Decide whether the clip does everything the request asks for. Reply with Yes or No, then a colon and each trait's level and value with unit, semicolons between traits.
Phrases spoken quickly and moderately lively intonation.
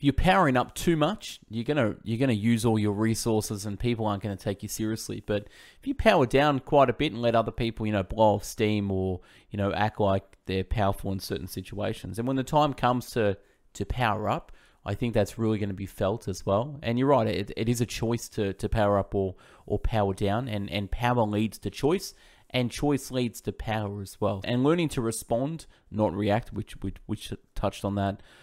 Yes: fast, 225 wpm; average, 3.3 semitones